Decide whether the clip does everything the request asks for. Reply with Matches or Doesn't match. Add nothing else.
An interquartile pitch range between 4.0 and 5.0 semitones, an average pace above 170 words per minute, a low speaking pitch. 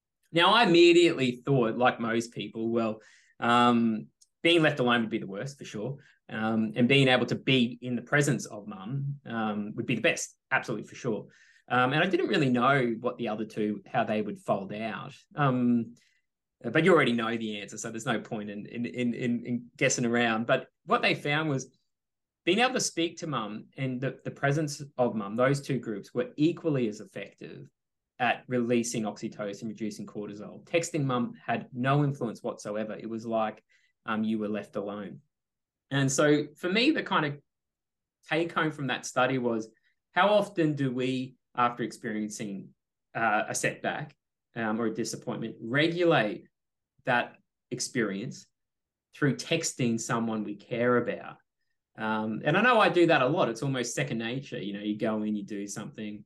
Matches